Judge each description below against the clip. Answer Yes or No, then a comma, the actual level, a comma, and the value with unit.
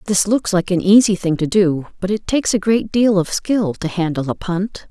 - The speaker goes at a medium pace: No, fast, 245 wpm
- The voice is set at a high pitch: Yes, high, 195 Hz